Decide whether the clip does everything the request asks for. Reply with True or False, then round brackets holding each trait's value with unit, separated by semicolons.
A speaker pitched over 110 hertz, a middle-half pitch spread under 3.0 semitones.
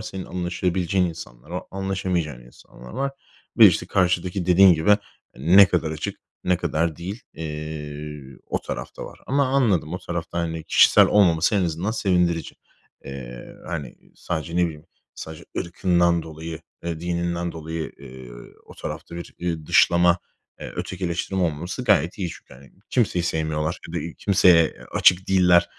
False (85 Hz; 2.5 semitones)